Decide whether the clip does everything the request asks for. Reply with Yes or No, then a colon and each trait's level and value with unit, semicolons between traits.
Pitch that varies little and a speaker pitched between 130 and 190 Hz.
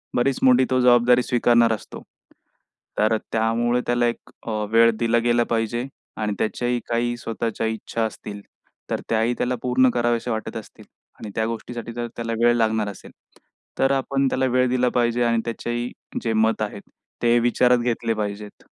No: narrow, 1.4 semitones; low, 120 Hz